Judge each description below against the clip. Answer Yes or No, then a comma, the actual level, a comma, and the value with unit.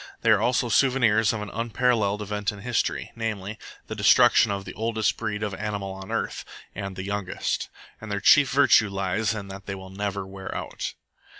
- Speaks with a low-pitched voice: Yes, low, 105 Hz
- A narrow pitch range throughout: Yes, narrow, 2.3 semitones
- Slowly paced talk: No, average, 190 wpm